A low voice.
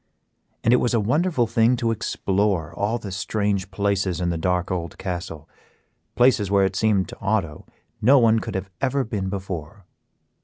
Yes: low, 100 Hz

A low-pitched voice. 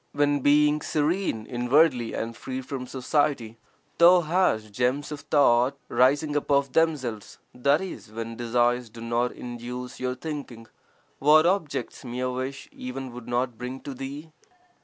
Yes: low, 130 Hz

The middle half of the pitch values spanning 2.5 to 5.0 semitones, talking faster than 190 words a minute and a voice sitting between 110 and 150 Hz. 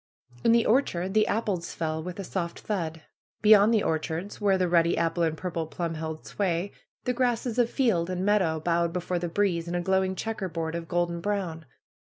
No: average, 3.6 semitones; average, 200 wpm; medium, 175 Hz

